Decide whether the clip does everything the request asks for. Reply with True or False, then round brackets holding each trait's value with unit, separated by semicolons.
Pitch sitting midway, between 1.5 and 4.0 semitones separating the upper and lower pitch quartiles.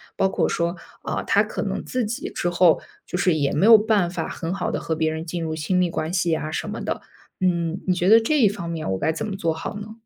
True (175 Hz; 3.6 semitones)